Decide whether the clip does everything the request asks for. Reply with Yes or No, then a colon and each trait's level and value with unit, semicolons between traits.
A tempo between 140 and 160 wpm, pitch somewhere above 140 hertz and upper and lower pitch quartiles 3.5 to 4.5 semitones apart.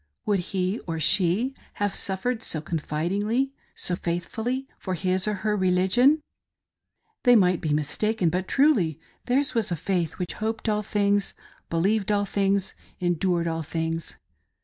Yes: average, 155 wpm; high, 190 Hz; average, 4.0 semitones